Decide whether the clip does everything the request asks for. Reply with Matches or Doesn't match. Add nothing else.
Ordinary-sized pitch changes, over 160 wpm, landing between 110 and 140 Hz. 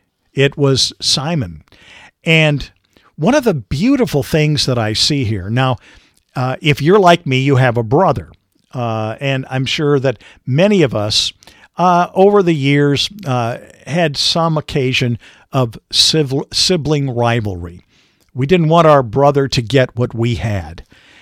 Doesn't match